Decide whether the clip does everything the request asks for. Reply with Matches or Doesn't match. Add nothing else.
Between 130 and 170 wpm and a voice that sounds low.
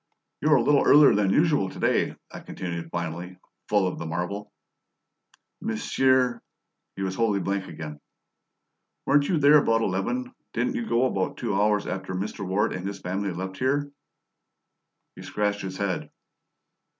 Matches